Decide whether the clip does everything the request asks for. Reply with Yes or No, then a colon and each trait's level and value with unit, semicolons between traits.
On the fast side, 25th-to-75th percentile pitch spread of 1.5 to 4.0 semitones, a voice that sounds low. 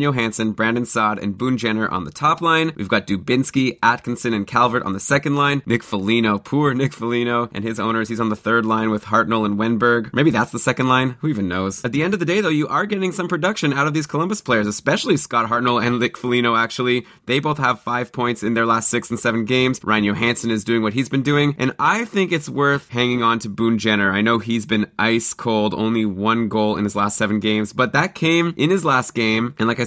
Yes: fast, 245 wpm; average, 3.2 semitones; low, 120 Hz